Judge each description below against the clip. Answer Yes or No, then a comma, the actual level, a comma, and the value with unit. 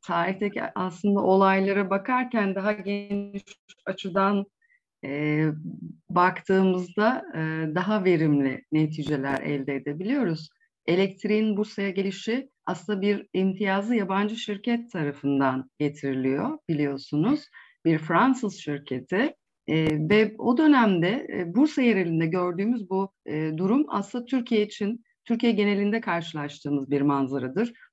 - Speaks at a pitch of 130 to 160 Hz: No, high, 195 Hz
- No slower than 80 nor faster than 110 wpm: Yes, average, 100 wpm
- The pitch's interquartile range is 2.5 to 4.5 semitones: No, wide, 5.5 semitones